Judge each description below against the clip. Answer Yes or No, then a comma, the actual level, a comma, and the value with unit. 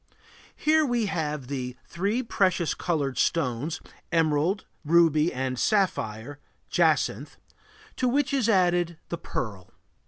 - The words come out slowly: Yes, slow, 115 wpm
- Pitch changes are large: Yes, wide, 6.0 semitones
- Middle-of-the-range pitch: Yes, medium, 170 Hz